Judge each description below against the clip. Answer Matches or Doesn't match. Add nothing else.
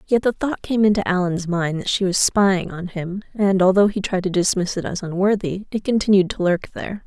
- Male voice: Doesn't match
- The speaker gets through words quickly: Matches